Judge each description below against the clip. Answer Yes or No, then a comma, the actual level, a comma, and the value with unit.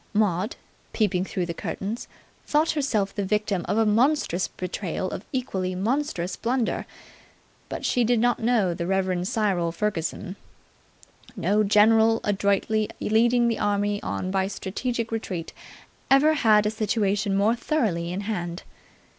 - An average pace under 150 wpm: Yes, average, 140 wpm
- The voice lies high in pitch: Yes, high, 210 Hz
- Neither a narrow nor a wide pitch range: Yes, average, 3.3 semitones